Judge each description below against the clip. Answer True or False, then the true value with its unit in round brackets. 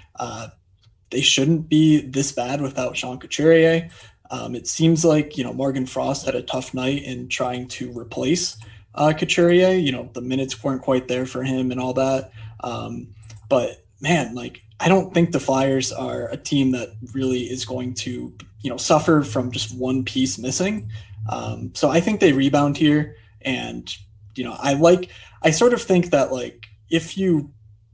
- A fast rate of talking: False (180 wpm)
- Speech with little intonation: False (3.7 semitones)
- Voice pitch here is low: True (130 Hz)